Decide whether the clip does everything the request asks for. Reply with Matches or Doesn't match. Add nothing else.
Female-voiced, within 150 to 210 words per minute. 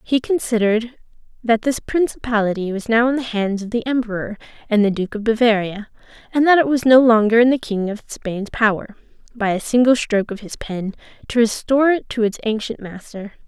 Matches